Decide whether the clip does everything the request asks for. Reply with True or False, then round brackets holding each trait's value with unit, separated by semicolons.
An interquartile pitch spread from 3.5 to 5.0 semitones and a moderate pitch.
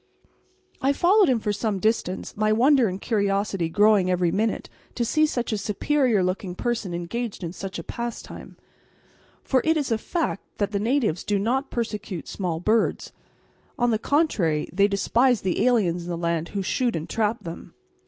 False (4.6 semitones; 210 Hz)